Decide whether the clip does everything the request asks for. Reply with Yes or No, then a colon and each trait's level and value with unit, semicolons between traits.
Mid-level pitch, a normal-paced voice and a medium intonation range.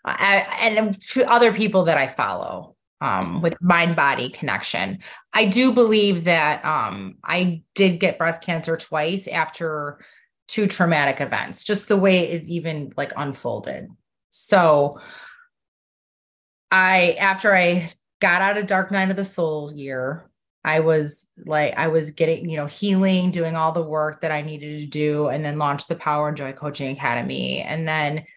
Yes: medium, 165 Hz; average, 160 wpm; average, 4.2 semitones